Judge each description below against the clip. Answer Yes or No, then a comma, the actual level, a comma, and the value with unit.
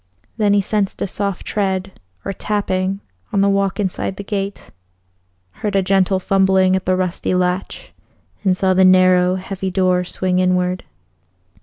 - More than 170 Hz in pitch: Yes, high, 190 Hz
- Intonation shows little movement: Yes, narrow, 1.2 semitones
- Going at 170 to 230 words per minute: No, average, 155 wpm